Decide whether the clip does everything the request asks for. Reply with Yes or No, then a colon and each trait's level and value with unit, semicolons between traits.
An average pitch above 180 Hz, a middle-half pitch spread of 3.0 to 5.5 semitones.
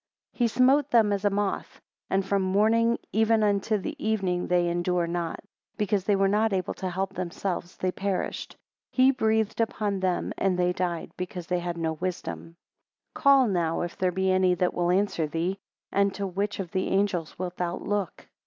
No: high, 190 Hz; narrow, 2.6 semitones